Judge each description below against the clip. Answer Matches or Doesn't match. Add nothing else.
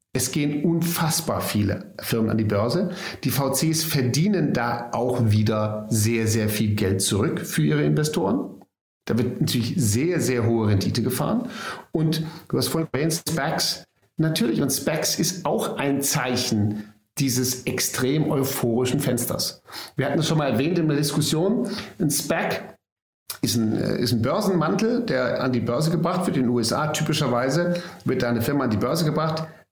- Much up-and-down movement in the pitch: Matches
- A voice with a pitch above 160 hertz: Doesn't match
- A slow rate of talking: Doesn't match